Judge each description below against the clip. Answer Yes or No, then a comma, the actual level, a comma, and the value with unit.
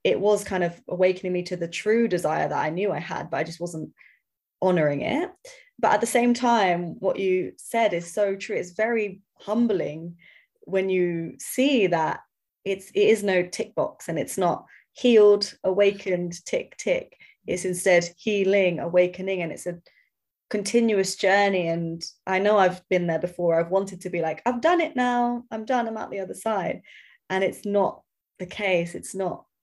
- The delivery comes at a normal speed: Yes, average, 185 wpm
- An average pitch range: Yes, average, 3.8 semitones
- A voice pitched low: No, high, 190 Hz